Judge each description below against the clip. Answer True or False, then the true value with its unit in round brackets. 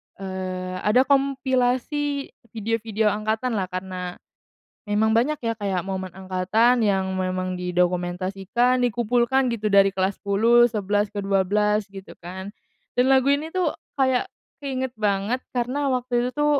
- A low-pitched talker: False (215 Hz)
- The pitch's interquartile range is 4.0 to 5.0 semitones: True (4.7 semitones)